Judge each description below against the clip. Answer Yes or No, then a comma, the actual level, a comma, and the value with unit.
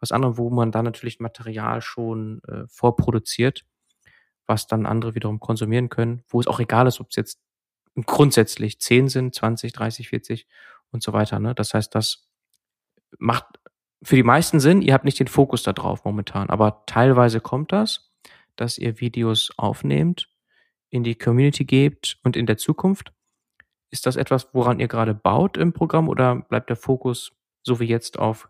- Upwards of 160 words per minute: Yes, average, 175 wpm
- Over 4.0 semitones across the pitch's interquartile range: No, average, 2.8 semitones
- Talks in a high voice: No, low, 120 Hz